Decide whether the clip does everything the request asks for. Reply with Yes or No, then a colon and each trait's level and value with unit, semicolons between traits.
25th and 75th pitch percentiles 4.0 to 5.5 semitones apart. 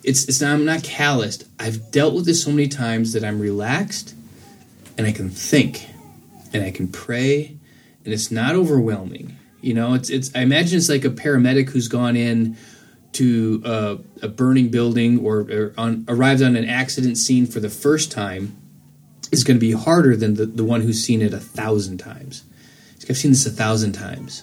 No: average, 3.6 semitones